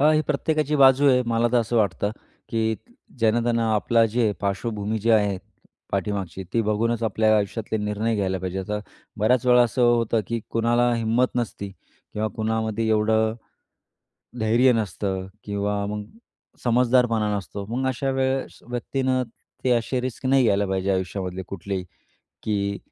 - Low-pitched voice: Yes, low, 110 Hz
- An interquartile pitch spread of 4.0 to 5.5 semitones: No, average, 2.9 semitones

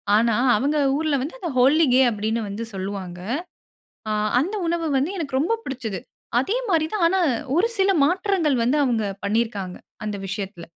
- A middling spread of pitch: No, wide, 7.7 semitones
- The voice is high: Yes, very high, 265 Hz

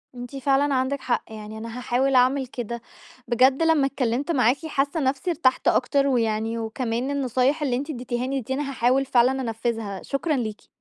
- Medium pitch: No, very high, 255 Hz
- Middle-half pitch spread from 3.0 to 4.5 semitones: No, narrow, 2.6 semitones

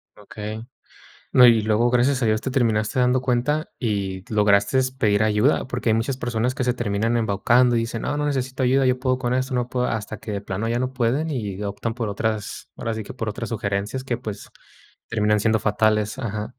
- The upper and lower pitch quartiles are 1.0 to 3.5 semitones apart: Yes, average, 3.1 semitones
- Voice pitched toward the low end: Yes, low, 115 Hz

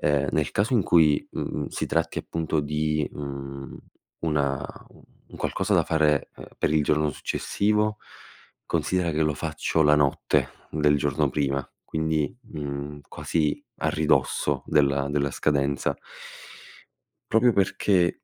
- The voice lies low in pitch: Yes, very low, 75 Hz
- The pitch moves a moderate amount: No, narrow, 2.2 semitones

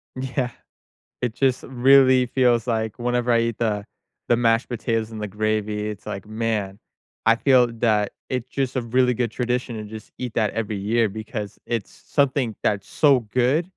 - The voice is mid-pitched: No, low, 115 Hz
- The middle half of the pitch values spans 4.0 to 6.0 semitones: No, average, 2.7 semitones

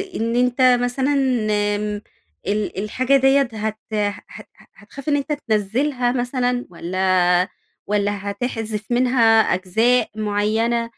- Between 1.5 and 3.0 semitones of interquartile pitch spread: No, average, 3.4 semitones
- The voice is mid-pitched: No, high, 225 Hz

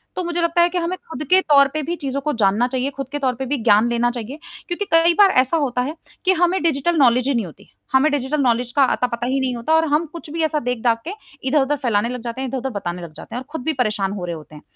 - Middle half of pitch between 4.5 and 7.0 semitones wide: Yes, average, 4.9 semitones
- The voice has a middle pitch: No, very high, 265 Hz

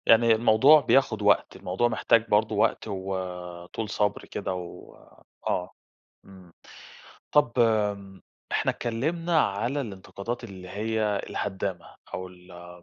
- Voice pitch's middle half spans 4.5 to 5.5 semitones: No, average, 3.7 semitones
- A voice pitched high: No, low, 105 Hz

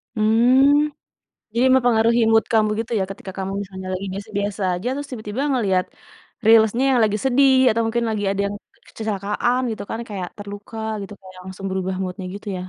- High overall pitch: Yes, high, 215 Hz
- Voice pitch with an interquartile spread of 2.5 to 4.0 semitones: Yes, average, 3.3 semitones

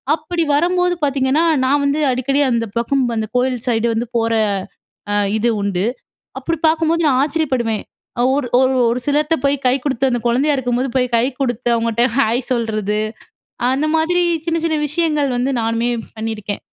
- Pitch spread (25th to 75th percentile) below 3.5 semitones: No, average, 4.4 semitones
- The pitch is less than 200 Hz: No, very high, 260 Hz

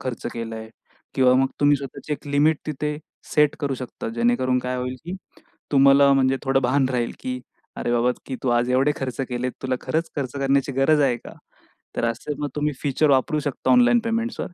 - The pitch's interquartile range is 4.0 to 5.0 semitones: No, narrow, 2.5 semitones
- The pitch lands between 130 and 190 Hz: Yes, low, 135 Hz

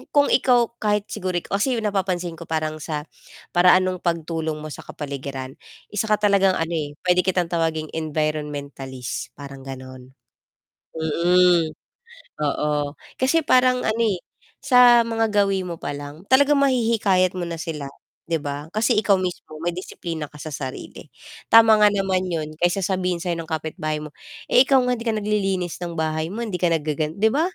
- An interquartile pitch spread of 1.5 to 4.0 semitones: No, average, 5.1 semitones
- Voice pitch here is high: No, medium, 175 Hz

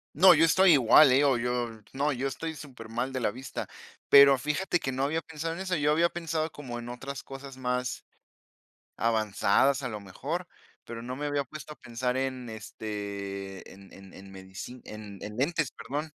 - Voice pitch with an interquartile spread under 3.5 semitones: No, average, 4.6 semitones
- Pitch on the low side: Yes, low, 130 Hz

